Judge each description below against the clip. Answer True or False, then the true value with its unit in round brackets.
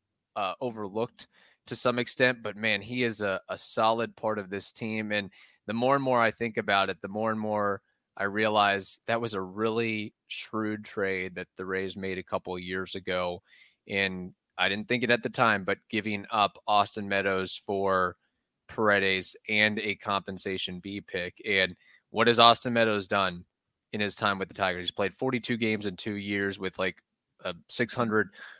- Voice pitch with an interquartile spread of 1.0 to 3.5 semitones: True (2.8 semitones)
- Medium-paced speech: True (185 wpm)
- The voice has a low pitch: True (105 Hz)